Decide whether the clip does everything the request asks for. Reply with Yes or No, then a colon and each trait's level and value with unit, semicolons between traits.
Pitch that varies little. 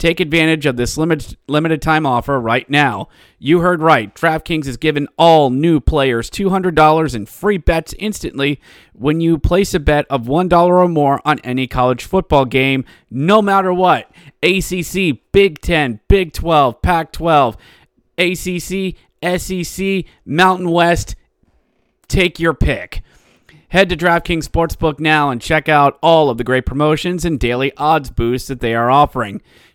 No: average, 4.5 semitones